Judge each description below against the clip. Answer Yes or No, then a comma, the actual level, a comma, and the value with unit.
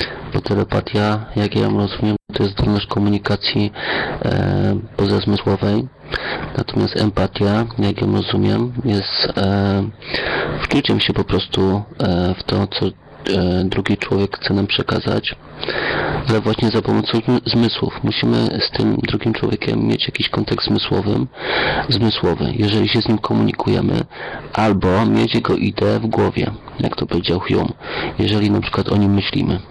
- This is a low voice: Yes, low, 105 Hz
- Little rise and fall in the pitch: Yes, narrow, 2.3 semitones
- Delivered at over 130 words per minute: Yes, average, 140 wpm